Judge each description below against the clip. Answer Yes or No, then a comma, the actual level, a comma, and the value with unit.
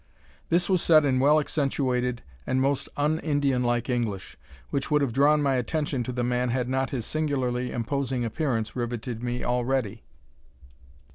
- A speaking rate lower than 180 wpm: Yes, average, 155 wpm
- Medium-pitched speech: No, low, 130 Hz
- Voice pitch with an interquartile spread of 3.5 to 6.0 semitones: No, average, 2.8 semitones